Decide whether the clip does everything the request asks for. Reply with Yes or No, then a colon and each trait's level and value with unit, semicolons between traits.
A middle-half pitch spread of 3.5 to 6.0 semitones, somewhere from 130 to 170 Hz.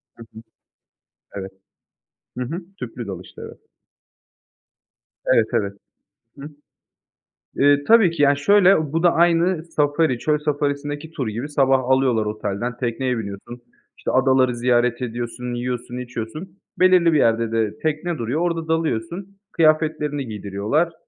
Yes: average, 5.2 semitones; low, 135 Hz